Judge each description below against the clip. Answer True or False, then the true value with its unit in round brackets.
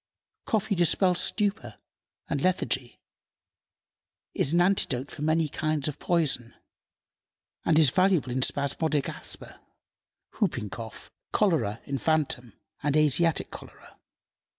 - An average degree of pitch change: True (4.8 semitones)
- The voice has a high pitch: False (155 Hz)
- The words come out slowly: True (105 wpm)